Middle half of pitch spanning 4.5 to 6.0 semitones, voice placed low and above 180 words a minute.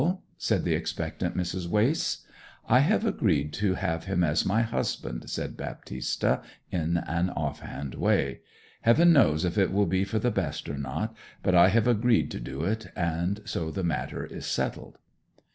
No: average, 5.1 semitones; very low, 95 Hz; average, 175 wpm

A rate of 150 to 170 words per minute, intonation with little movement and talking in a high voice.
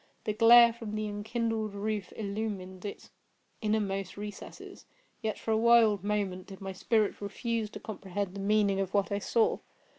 Yes: average, 160 wpm; narrow, 1.9 semitones; high, 210 Hz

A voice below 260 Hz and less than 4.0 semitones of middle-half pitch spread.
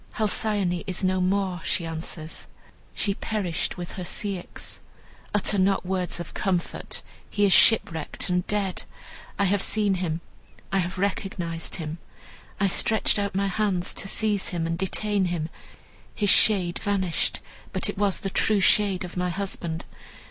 Yes: high, 190 Hz; narrow, 2.4 semitones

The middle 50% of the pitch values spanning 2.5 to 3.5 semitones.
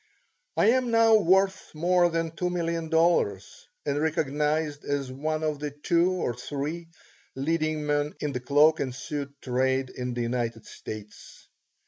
No: average, 3.9 semitones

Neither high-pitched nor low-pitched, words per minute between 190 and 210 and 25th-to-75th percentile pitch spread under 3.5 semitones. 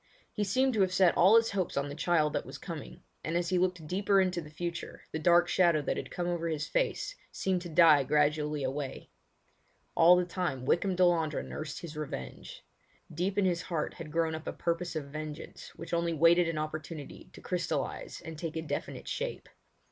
Yes: medium, 170 Hz; average, 200 wpm; average, 2.7 semitones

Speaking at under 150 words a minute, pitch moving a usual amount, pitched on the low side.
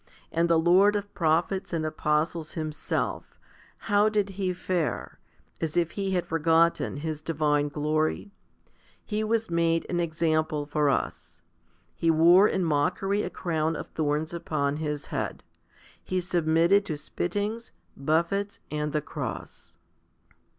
No: slow, 135 wpm; average, 3.2 semitones; medium, 165 Hz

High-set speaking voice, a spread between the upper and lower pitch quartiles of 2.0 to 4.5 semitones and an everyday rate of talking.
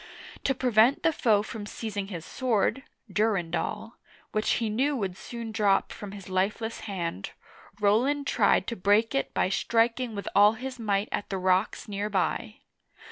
Yes: high, 215 Hz; average, 2.8 semitones; average, 160 wpm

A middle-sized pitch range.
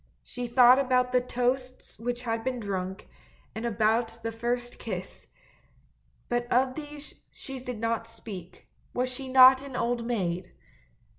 No: narrow, 2.1 semitones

